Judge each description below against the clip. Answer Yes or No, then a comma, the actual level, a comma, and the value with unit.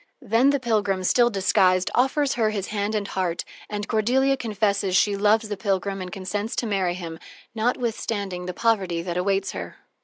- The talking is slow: No, average, 175 wpm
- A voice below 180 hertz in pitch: No, high, 205 Hz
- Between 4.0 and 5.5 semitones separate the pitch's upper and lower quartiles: No, average, 3.2 semitones